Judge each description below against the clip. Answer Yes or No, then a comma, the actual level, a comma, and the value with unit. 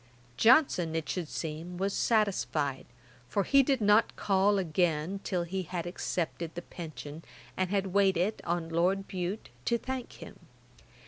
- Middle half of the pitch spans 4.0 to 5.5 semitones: No, average, 3.3 semitones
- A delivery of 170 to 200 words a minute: No, average, 145 wpm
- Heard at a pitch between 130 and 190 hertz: Yes, medium, 185 Hz